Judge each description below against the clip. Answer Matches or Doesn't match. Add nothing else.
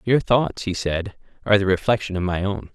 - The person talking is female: Doesn't match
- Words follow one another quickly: Matches